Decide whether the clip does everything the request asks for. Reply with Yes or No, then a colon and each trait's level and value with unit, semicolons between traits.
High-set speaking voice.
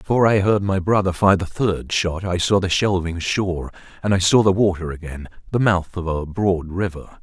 No: very low, 95 Hz